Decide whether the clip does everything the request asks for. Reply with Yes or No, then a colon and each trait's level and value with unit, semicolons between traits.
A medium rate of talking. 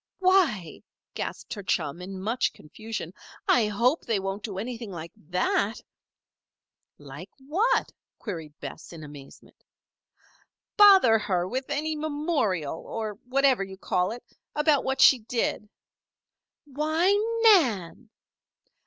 No: slow, 120 wpm